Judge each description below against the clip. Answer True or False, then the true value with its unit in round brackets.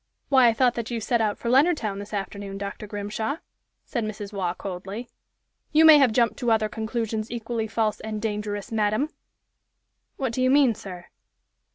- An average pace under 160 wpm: False (175 wpm)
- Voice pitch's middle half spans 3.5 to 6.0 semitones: False (2.7 semitones)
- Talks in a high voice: True (220 Hz)